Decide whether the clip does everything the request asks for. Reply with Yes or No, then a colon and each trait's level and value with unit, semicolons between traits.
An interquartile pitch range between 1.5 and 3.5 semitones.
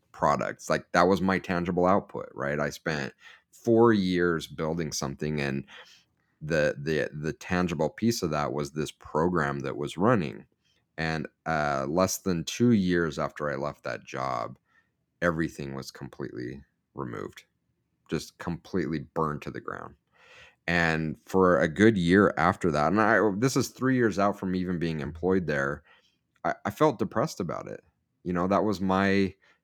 No: average, 4.8 semitones